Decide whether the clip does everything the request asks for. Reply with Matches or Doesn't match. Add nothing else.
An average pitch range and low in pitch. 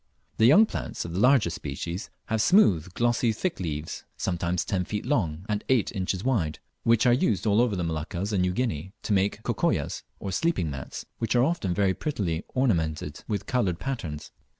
Doesn't match